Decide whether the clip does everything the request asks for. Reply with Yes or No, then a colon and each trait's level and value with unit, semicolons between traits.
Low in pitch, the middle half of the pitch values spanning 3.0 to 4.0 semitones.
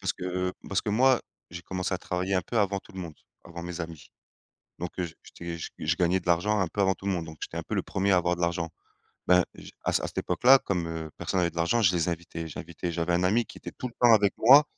No: very low, 90 Hz; narrow, 2.5 semitones